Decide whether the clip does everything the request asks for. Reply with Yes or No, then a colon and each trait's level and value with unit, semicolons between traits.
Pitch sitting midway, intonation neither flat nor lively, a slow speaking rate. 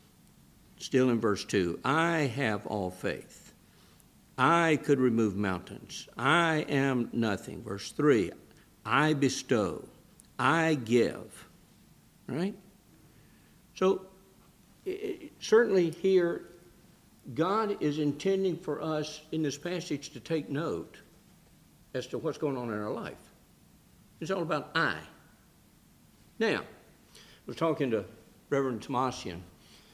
No: medium, 150 Hz; wide, 5.8 semitones; slow, 110 wpm